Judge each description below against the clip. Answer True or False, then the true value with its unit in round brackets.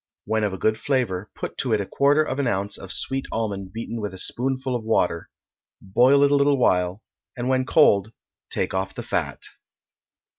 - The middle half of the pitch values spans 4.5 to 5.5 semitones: True (5.1 semitones)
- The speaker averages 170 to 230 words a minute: True (195 wpm)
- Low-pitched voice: True (115 Hz)